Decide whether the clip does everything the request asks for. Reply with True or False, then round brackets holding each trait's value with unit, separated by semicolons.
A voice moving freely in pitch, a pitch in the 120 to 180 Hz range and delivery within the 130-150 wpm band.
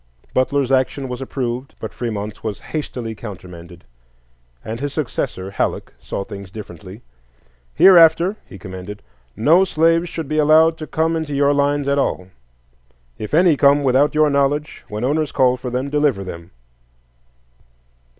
True (6.1 semitones; 135 Hz; 145 wpm)